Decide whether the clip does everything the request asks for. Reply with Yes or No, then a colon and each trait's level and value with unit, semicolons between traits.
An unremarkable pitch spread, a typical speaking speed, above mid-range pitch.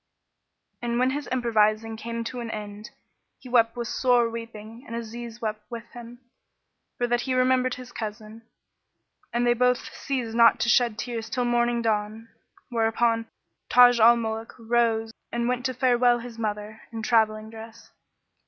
No: narrow, 1.5 semitones; average, 160 wpm; high, 235 Hz